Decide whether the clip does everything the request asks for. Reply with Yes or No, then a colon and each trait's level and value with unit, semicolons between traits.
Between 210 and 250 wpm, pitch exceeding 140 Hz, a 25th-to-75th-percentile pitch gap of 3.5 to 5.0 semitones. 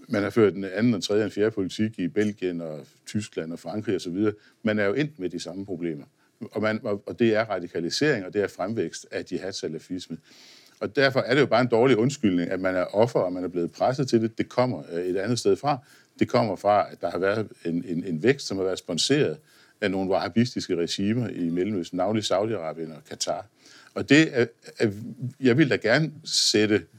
No: average, 220 wpm; low, 105 Hz; average, 4.5 semitones